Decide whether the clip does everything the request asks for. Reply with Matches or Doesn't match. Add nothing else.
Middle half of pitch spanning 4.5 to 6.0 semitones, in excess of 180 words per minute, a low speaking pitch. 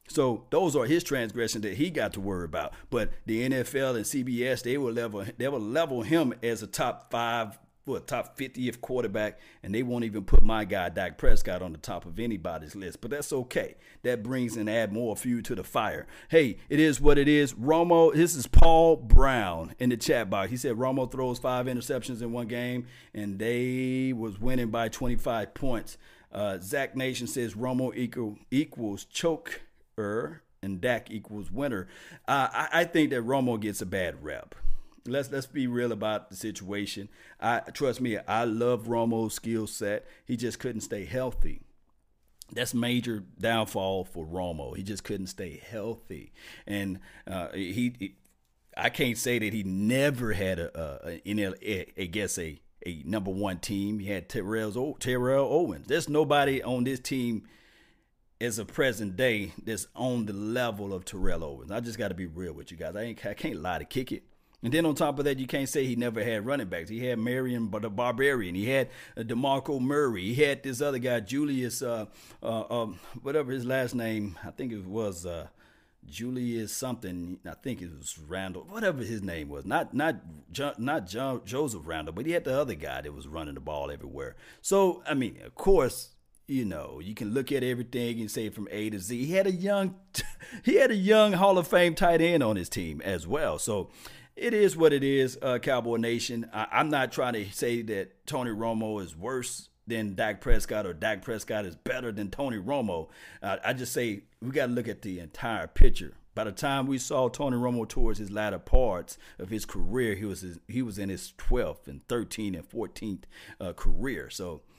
Doesn't match